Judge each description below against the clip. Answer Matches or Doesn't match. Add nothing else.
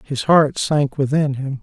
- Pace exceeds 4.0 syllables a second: Doesn't match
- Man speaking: Matches